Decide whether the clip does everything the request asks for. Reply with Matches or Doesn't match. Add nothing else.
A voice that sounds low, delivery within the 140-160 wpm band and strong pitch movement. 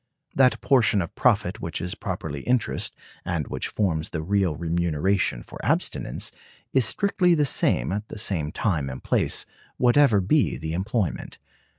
Matches